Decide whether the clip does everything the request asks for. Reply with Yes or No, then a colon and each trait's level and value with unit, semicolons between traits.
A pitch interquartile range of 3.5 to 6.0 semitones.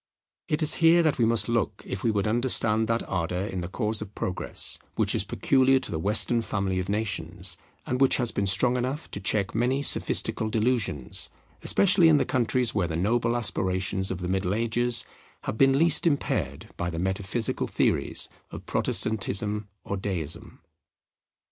Yes: average, 4.5 semitones